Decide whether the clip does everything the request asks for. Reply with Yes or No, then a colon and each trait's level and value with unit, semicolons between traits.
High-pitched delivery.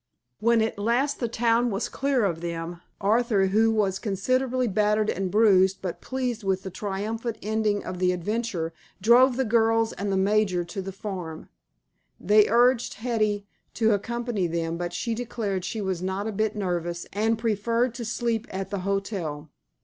Yes: high, 210 Hz